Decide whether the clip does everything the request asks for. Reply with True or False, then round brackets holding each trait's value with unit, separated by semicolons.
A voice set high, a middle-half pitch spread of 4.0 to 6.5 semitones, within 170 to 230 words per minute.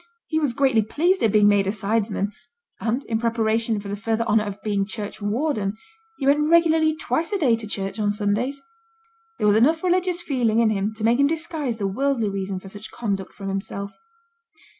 True (225 Hz; 5.5 semitones; 195 wpm)